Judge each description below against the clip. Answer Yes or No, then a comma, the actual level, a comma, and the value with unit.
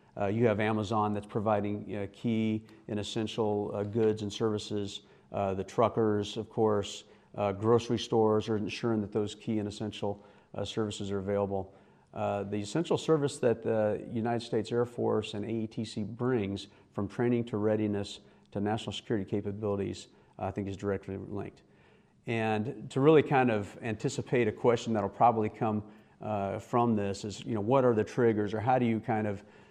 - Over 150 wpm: Yes, average, 180 wpm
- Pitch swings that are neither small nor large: No, narrow, 1.9 semitones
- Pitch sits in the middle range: No, low, 105 Hz